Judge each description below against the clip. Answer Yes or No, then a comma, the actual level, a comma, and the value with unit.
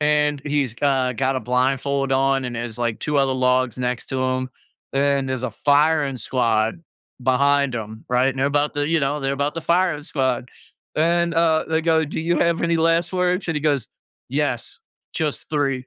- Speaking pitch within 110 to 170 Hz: Yes, medium, 140 Hz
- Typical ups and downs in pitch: Yes, average, 3.2 semitones